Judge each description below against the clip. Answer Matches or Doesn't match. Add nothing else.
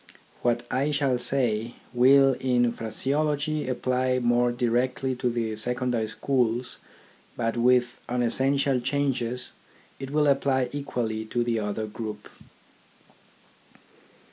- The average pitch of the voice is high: Doesn't match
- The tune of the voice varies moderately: Doesn't match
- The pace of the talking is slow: Matches